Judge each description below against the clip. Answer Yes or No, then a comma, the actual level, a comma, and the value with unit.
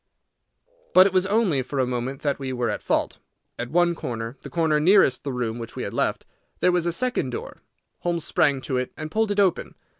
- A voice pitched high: No, medium, 150 Hz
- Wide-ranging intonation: Yes, wide, 5.8 semitones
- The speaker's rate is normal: No, fast, 220 wpm